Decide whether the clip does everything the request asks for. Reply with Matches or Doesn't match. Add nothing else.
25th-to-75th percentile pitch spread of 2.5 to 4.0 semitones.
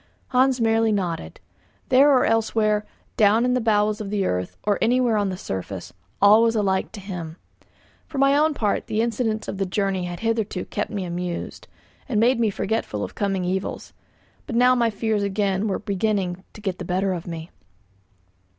Matches